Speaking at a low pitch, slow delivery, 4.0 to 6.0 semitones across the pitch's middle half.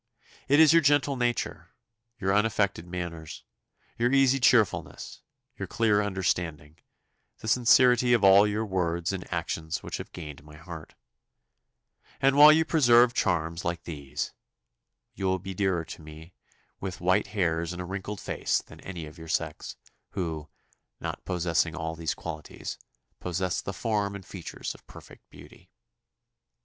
No: very low, 95 Hz; average, 150 wpm; average, 4.9 semitones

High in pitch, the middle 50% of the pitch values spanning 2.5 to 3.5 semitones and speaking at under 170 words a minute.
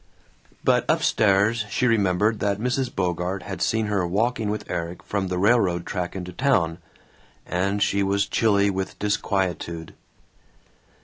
No: low, 100 Hz; average, 2.9 semitones; average, 140 wpm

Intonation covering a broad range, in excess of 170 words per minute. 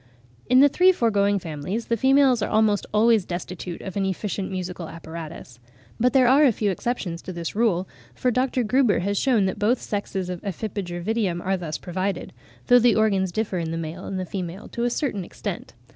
No: average, 4.7 semitones; average, 195 wpm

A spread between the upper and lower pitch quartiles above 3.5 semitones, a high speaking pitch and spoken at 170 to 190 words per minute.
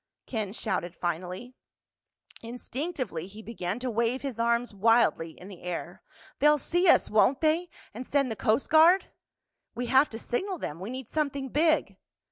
No: wide, 5.4 semitones; high, 240 Hz; average, 155 wpm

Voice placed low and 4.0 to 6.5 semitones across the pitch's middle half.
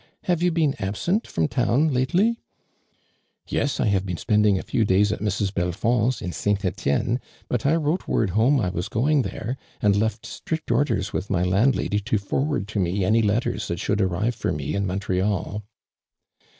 Yes: low, 105 Hz; average, 5.1 semitones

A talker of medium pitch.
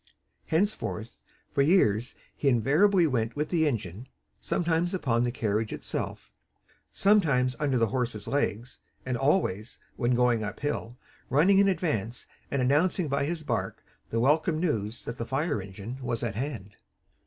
No: low, 130 Hz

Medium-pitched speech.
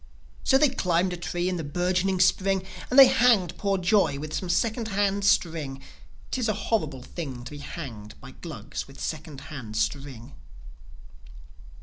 Yes: medium, 175 Hz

